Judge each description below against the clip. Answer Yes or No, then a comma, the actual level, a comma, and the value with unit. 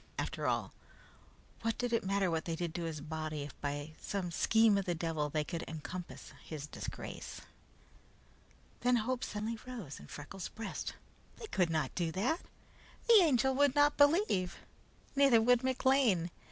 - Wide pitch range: Yes, wide, 7.5 semitones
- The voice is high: Yes, high, 195 Hz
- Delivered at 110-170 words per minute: Yes, average, 165 wpm